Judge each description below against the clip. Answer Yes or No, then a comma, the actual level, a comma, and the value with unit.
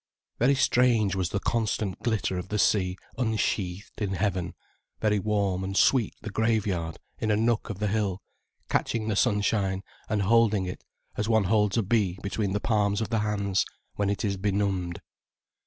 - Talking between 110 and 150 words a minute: No, average, 170 wpm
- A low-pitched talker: Yes, low, 105 Hz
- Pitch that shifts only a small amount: Yes, narrow, 2.3 semitones